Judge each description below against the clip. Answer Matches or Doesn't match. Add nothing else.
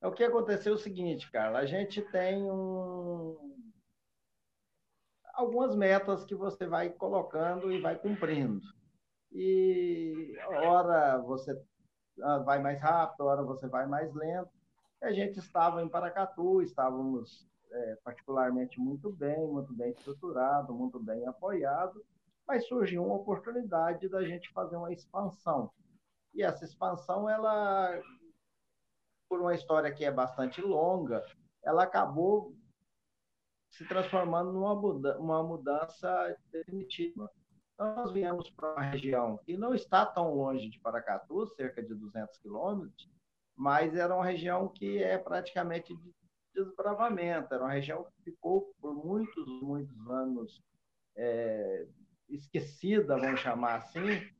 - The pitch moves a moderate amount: Doesn't match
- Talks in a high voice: Doesn't match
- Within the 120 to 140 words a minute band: Matches